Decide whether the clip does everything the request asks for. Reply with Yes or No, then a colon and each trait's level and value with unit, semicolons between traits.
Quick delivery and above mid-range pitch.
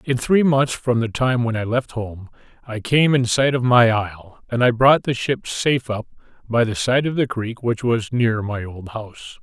No: fast, 230 wpm; low, 120 Hz